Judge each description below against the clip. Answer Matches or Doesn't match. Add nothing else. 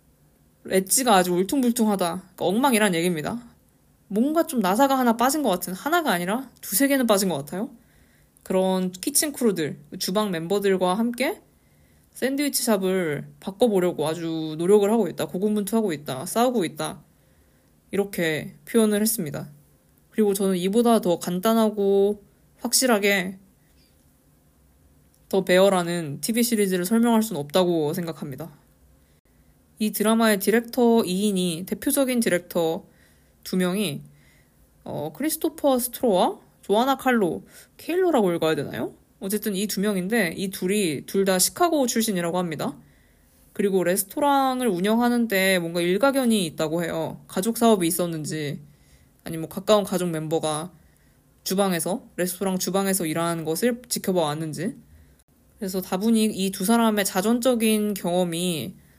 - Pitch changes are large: Doesn't match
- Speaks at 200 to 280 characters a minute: Doesn't match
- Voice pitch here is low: Doesn't match